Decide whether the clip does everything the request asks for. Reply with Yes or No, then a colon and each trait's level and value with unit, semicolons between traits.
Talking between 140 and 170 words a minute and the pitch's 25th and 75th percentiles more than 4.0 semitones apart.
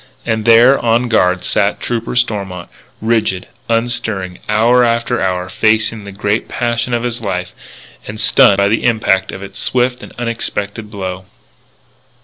No: average, 150 wpm; average, 3.1 semitones